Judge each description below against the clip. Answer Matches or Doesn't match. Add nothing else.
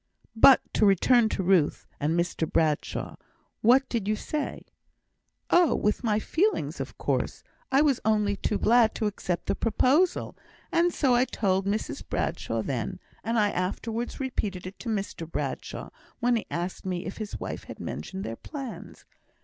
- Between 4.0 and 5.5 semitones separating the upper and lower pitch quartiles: Matches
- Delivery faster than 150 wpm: Matches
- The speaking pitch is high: Matches